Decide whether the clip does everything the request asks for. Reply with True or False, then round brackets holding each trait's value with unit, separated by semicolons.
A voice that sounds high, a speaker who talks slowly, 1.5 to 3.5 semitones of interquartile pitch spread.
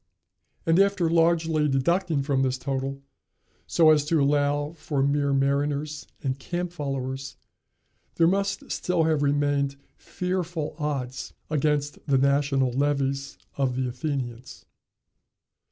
False (145 Hz; 120 wpm; 2.8 semitones)